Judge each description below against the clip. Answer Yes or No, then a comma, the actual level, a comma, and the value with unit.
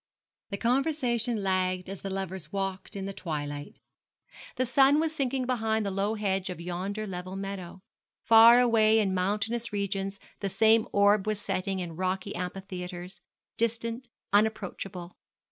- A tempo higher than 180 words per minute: No, average, 145 wpm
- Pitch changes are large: No, average, 3.1 semitones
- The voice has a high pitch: Yes, high, 200 Hz